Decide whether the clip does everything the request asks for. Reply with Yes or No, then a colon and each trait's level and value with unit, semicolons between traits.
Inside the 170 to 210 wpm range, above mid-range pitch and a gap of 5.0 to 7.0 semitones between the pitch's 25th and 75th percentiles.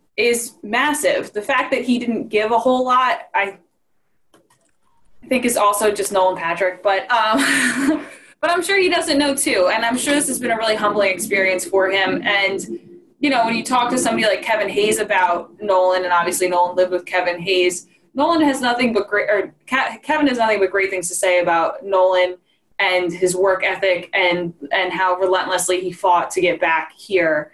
Yes: average, 195 wpm; high, 200 Hz; wide, 5.6 semitones